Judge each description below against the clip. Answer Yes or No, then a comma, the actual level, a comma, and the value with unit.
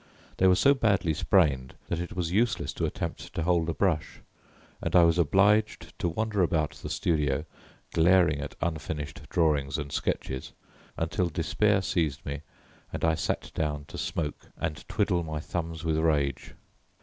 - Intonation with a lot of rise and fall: No, average, 3.2 semitones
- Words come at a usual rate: Yes, average, 160 wpm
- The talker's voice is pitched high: No, very low, 80 Hz